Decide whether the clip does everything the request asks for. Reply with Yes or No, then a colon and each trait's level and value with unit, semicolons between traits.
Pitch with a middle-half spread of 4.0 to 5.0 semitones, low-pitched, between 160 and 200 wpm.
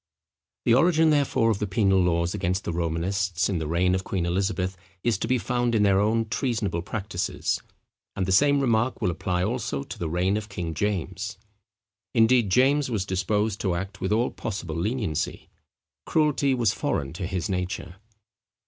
Yes: average, 4.3 semitones; low, 100 Hz; average, 175 wpm